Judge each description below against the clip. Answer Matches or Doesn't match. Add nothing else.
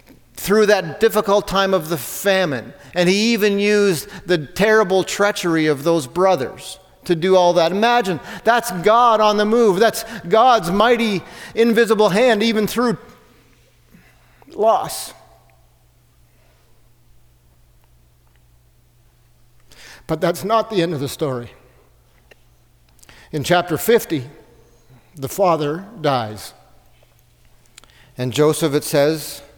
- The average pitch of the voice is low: Doesn't match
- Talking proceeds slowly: Matches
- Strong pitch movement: Matches